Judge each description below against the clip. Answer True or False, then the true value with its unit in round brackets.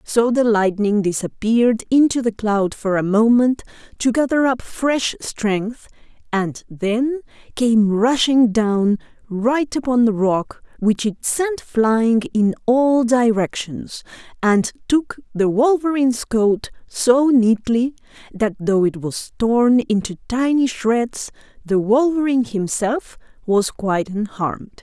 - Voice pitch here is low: False (230 Hz)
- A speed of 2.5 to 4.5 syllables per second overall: True (3.7 syllables/s)